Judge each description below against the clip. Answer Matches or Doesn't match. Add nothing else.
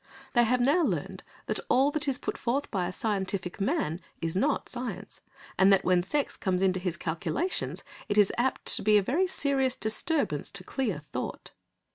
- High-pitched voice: Matches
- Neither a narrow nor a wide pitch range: Doesn't match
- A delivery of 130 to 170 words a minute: Doesn't match